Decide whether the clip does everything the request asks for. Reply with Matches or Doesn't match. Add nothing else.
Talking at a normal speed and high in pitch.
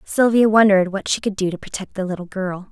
Doesn't match